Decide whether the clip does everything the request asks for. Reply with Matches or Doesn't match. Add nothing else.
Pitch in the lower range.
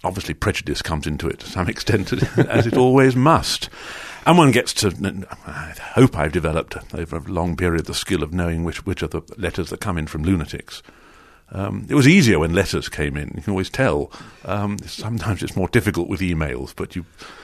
Matches